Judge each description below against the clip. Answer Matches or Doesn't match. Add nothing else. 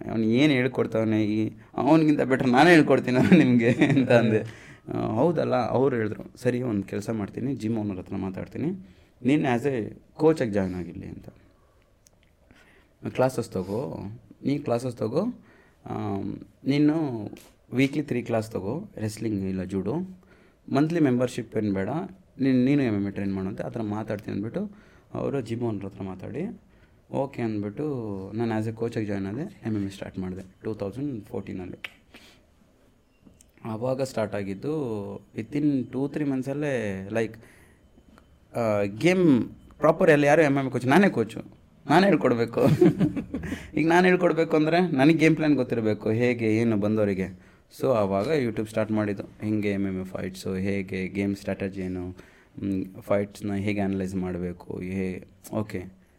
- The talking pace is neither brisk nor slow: Doesn't match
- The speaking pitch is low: Matches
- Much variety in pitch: Doesn't match